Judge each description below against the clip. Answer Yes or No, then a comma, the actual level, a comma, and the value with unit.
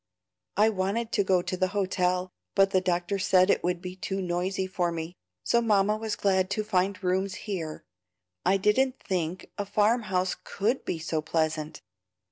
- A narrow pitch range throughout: Yes, narrow, 2.1 semitones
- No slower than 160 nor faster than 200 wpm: Yes, average, 175 wpm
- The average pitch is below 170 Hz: No, high, 190 Hz